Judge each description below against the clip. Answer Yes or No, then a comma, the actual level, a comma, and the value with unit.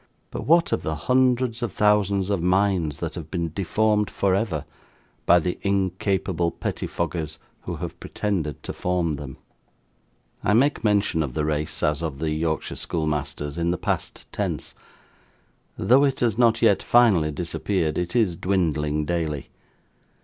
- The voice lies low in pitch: Yes, very low, 90 Hz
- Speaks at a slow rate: No, average, 150 wpm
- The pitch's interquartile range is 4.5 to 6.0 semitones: Yes, average, 5.0 semitones